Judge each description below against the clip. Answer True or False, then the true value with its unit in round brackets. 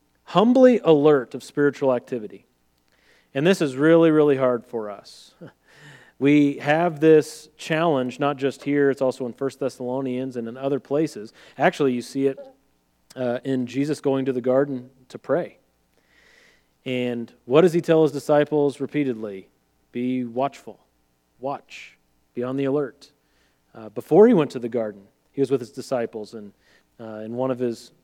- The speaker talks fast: False (160 wpm)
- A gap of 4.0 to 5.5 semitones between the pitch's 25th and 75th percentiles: False (3.6 semitones)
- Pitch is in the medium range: False (130 Hz)